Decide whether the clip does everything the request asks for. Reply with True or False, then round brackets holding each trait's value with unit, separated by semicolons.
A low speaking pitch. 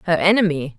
False (170 Hz)